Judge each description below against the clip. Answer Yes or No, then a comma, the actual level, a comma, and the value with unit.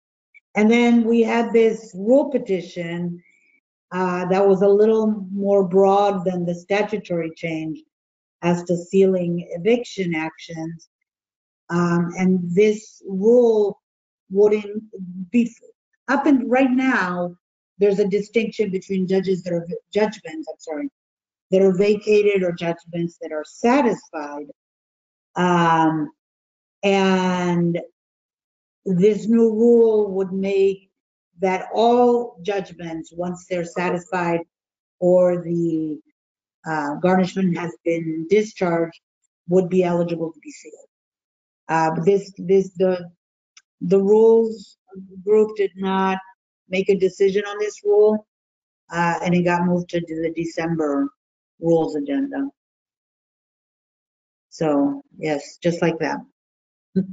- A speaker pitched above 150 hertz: Yes, high, 190 Hz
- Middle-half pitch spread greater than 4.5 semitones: No, average, 3.7 semitones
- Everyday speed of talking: No, slow, 115 wpm